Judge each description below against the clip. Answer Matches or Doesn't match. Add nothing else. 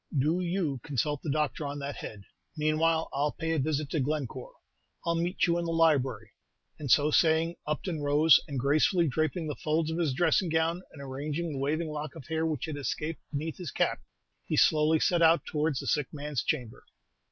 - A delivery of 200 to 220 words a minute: Matches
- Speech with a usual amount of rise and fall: Doesn't match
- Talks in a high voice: Doesn't match